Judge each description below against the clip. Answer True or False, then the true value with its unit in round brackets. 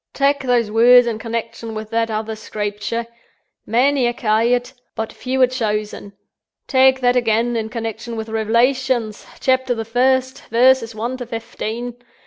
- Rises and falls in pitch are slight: True (2.3 semitones)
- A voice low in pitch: False (235 Hz)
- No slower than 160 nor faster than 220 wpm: False (145 wpm)